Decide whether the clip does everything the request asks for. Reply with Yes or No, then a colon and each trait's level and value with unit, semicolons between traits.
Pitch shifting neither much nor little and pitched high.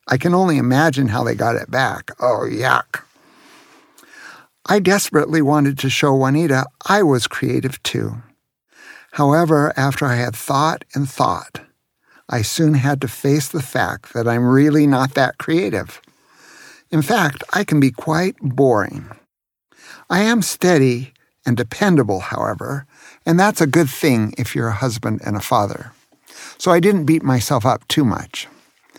No: average, 4.0 semitones; medium, 140 Hz